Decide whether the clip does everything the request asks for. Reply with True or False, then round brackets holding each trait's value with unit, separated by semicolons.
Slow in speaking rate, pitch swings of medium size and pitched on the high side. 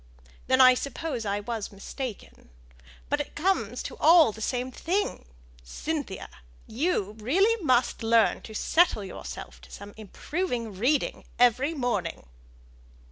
False (130 wpm; 6.1 semitones; 250 Hz)